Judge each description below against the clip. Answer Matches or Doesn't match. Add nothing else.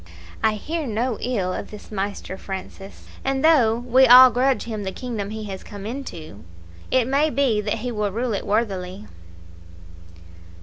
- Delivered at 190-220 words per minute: Doesn't match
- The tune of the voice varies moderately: Matches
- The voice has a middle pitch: Doesn't match